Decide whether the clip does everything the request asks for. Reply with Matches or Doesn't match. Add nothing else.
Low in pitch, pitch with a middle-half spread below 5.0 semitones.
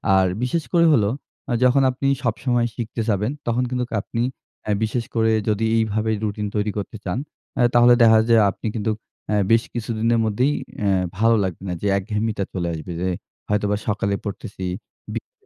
Matches